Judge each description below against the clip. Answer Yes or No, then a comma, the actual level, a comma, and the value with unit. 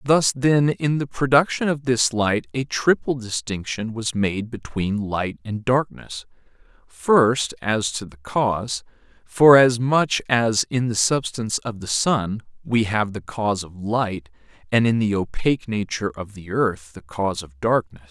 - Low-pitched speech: Yes, low, 110 Hz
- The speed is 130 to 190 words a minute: Yes, average, 160 wpm